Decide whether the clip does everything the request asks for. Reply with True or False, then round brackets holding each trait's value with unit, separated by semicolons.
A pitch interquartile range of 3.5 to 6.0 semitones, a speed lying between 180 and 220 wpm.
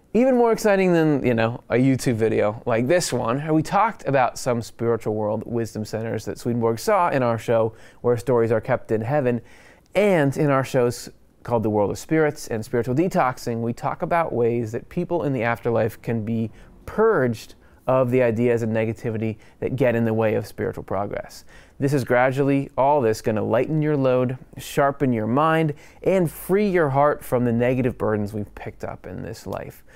True (4.4 semitones; 190 wpm)